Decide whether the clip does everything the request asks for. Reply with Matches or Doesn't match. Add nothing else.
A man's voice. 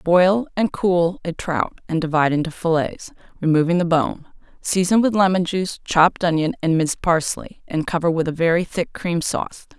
Doesn't match